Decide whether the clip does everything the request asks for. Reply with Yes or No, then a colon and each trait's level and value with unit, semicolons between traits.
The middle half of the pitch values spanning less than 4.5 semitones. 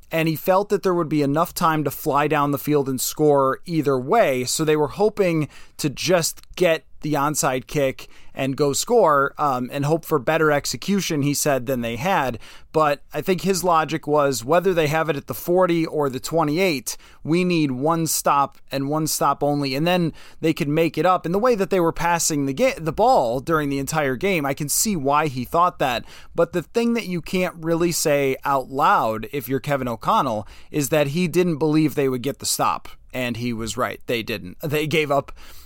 Yes: average, 3.4 semitones